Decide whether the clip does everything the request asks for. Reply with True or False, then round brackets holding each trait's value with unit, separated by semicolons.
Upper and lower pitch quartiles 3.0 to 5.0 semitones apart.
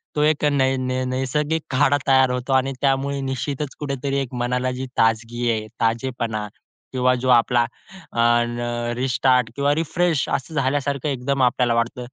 False (2.4 semitones)